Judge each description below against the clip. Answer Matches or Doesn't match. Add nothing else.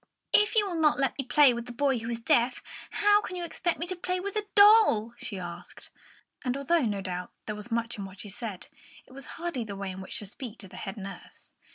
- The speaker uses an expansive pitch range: Matches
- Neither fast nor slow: Doesn't match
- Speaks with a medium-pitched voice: Doesn't match